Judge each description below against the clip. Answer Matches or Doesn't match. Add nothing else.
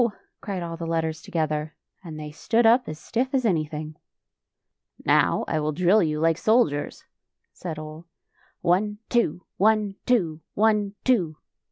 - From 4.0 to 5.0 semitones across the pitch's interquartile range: Doesn't match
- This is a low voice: Doesn't match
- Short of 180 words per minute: Matches